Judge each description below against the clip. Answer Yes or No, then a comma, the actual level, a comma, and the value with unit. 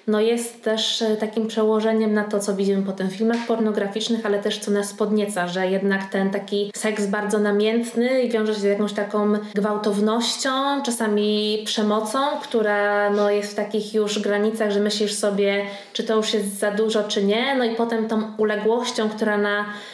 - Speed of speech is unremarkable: No, fast, 175 wpm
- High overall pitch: Yes, high, 215 Hz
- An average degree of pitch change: No, narrow, 1.3 semitones